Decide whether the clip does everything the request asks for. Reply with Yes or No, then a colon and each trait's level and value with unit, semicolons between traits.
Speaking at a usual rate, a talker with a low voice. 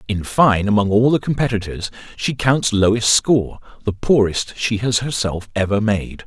Yes: average, 155 wpm; low, 110 Hz